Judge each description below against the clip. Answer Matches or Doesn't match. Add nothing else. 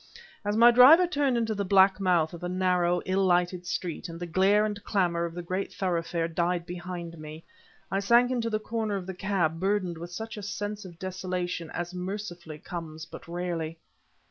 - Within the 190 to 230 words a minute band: Matches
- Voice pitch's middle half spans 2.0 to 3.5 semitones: Matches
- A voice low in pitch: Doesn't match